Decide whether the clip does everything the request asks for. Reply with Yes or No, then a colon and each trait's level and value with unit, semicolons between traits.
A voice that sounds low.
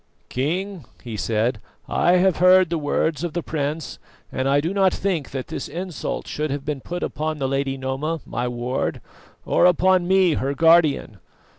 No: medium, 155 Hz